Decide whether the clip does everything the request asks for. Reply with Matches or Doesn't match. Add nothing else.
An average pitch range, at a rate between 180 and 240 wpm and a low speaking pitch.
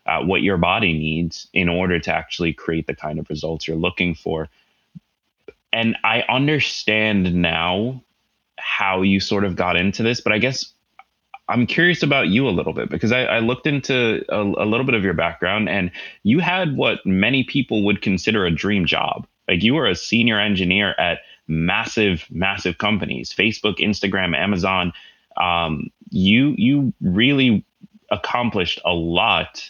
Doesn't match